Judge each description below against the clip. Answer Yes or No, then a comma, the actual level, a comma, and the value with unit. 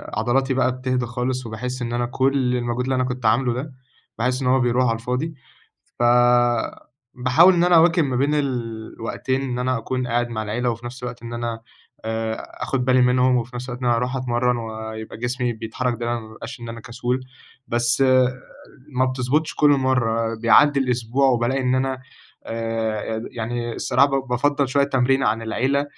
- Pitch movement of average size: No, narrow, 1.9 semitones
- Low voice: Yes, low, 125 Hz